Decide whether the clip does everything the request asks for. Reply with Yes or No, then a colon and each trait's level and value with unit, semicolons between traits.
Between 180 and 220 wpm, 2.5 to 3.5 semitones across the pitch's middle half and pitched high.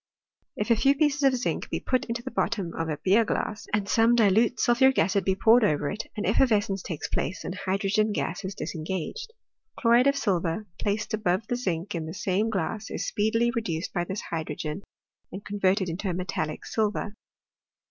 No: average, 190 wpm; average, 3.9 semitones; high, 205 Hz